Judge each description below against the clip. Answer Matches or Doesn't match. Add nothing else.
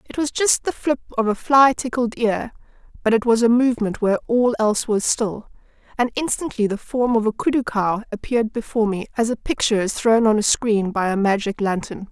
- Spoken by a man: Doesn't match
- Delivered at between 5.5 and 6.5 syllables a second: Matches